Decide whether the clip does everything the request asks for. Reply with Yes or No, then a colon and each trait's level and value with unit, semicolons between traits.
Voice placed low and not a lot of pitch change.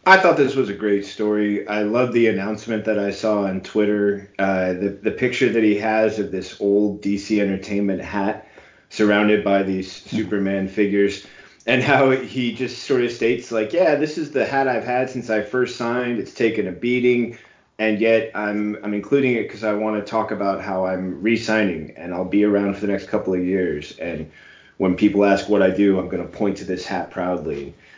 Yes: low, 105 Hz; narrow, 2.2 semitones